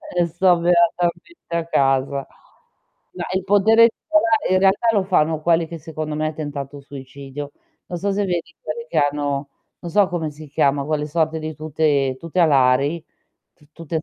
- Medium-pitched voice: Yes, medium, 160 Hz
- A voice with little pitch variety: No, average, 3.7 semitones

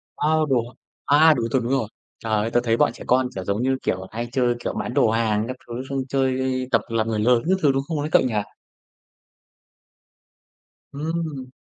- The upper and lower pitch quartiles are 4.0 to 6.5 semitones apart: No, average, 3.2 semitones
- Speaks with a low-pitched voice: Yes, low, 125 Hz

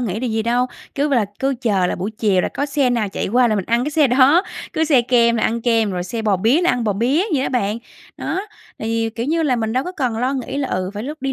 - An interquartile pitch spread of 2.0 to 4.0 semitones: Yes, average, 3.7 semitones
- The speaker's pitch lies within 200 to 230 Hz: No, high, 240 Hz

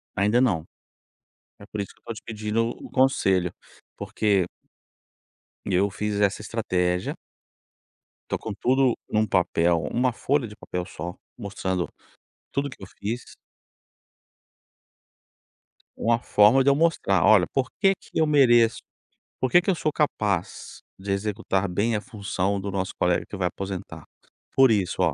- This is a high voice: No, low, 105 Hz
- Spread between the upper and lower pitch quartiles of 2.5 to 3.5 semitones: No, average, 4.3 semitones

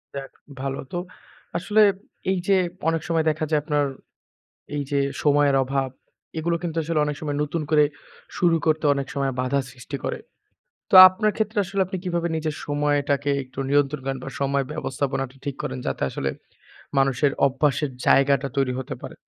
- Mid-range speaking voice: Yes, medium, 145 Hz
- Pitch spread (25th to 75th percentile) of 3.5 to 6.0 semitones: No, narrow, 2.6 semitones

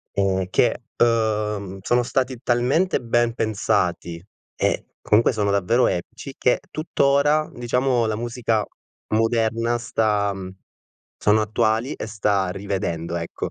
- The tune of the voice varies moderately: Yes, average, 3.0 semitones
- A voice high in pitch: No, low, 110 Hz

